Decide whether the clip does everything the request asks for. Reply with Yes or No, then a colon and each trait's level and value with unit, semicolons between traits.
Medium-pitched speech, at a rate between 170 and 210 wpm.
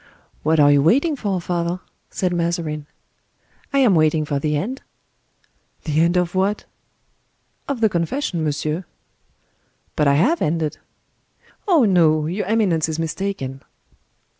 No: medium, 170 Hz; slow, 135 wpm